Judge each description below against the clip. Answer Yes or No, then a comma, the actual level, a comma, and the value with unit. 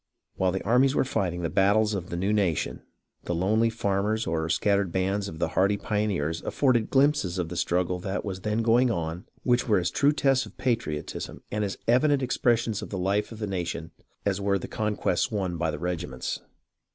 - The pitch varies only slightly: No, average, 4.2 semitones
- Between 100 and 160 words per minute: No, fast, 205 wpm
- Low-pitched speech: Yes, low, 100 Hz